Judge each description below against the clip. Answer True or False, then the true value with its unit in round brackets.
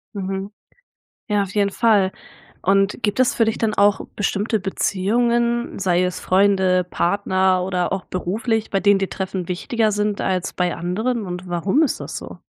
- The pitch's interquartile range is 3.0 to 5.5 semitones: False (2.5 semitones)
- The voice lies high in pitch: True (195 Hz)